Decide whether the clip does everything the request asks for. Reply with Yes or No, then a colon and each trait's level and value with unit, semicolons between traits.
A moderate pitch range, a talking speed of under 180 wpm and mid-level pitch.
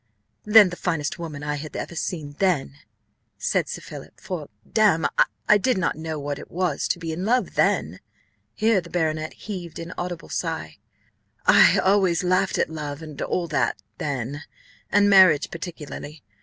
Yes: average, 3.7 semitones; average, 165 wpm; medium, 165 Hz